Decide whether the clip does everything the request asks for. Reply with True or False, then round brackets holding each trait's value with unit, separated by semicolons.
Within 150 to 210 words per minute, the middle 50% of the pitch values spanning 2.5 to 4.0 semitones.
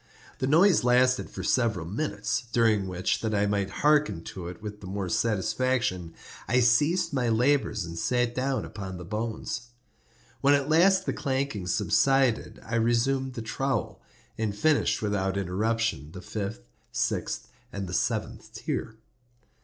False (155 wpm; 4.8 semitones)